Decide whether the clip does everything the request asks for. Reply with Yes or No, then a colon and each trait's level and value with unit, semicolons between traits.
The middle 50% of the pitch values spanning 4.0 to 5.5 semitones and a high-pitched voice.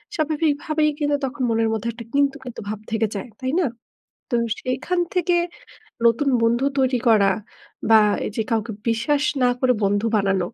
Yes: average, 4.6 semitones; very high, 250 Hz